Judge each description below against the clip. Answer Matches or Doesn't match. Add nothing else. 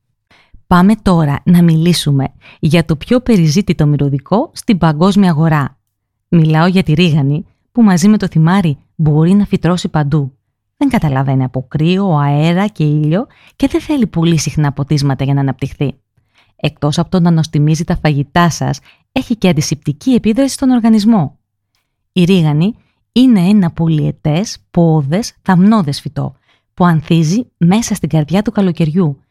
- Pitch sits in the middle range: Matches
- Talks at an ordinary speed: Matches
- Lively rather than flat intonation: Doesn't match